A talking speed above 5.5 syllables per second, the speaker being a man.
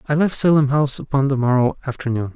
Yes: 6.5 syllables/s; male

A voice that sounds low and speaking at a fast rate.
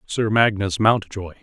No: low, 105 Hz; slow, 125 wpm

